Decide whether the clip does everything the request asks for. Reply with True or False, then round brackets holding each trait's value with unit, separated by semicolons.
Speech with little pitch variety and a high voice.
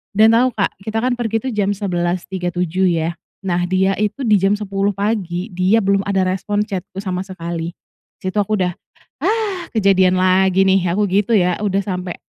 True (2.3 semitones; 195 Hz)